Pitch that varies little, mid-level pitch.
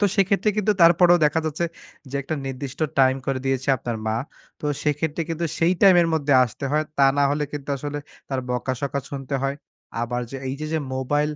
No: average, 3.5 semitones; medium, 145 Hz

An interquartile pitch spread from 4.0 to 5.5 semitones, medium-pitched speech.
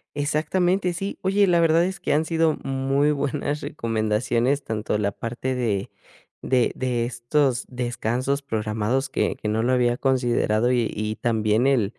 No: average, 4.3 semitones; low, 125 Hz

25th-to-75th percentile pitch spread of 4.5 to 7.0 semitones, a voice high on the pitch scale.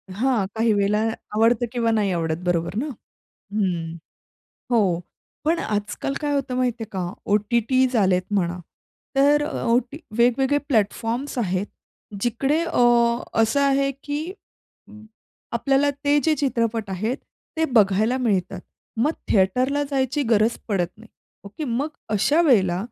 Yes: average, 4.9 semitones; high, 230 Hz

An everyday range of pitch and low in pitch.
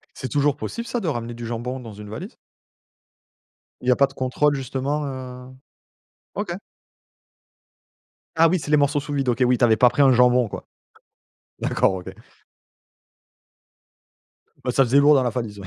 Yes: average, 3.0 semitones; low, 130 Hz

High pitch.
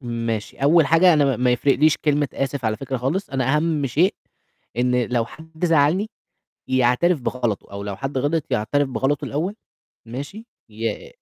No: low, 135 Hz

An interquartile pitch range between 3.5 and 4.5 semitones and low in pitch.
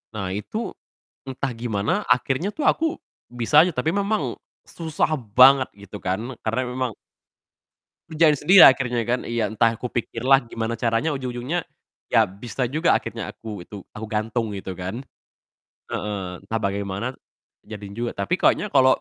Yes: average, 4.0 semitones; low, 120 Hz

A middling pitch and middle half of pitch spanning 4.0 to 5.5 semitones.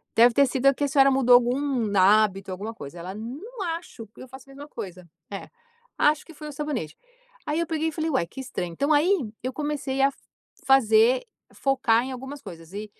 No: very high, 265 Hz; average, 5.1 semitones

